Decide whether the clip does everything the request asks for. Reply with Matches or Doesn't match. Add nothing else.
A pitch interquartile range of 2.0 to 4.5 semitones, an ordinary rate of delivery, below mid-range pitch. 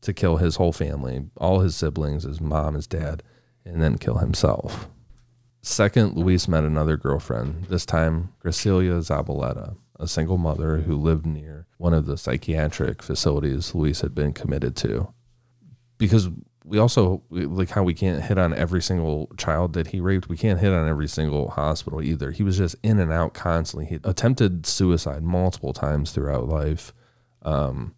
Matches